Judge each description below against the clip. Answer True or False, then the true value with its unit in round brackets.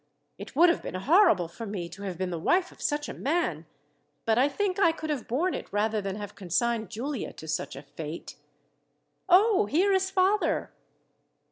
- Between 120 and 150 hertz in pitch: False (245 Hz)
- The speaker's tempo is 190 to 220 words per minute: True (195 wpm)